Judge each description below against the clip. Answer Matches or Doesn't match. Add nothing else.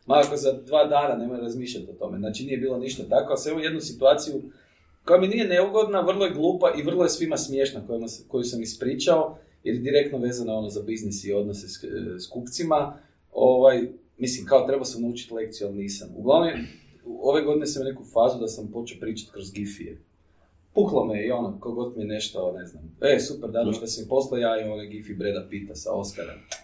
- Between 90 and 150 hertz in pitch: Matches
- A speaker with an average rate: Doesn't match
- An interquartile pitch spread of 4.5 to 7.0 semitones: Matches